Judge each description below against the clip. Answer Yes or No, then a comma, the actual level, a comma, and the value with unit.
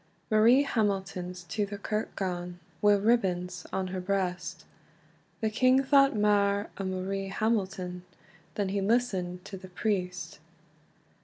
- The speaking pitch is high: Yes, high, 195 Hz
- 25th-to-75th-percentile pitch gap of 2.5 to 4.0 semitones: Yes, average, 2.8 semitones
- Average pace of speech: No, slow, 130 wpm